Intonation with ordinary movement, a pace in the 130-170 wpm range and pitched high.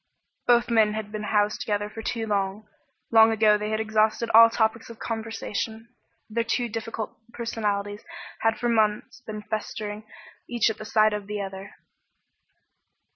No: narrow, 1.4 semitones; average, 155 wpm; high, 220 Hz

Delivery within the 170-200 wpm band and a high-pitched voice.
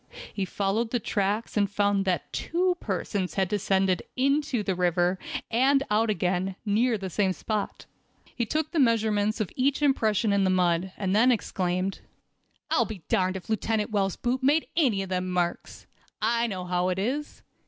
Yes: average, 175 wpm; high, 205 Hz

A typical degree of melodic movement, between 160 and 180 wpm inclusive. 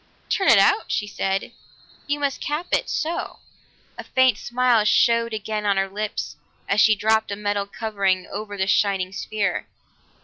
Yes: average, 3.0 semitones; average, 165 wpm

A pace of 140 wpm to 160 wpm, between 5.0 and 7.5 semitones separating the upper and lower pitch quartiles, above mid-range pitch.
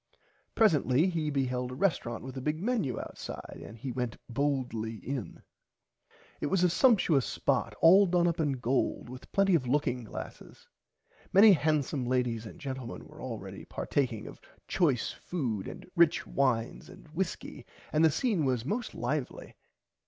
No: average, 155 wpm; wide, 5.5 semitones; medium, 140 Hz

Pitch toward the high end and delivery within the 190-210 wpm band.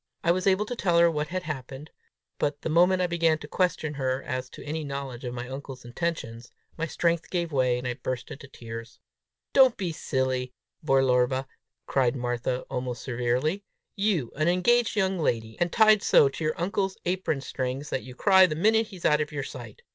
No: medium, 150 Hz; average, 195 wpm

